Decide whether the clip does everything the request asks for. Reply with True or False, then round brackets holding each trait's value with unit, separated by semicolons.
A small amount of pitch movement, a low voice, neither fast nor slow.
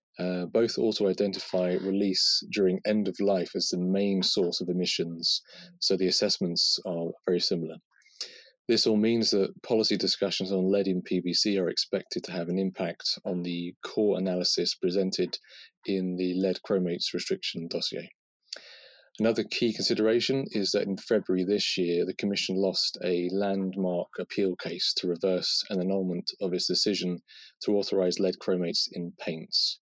True (1.8 semitones; 95 Hz; 155 wpm)